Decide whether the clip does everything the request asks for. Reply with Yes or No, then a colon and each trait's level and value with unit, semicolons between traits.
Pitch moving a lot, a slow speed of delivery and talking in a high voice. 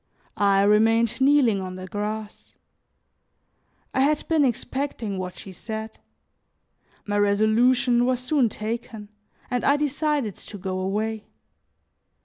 No: average, 3.9 semitones; slow, 120 wpm; high, 220 Hz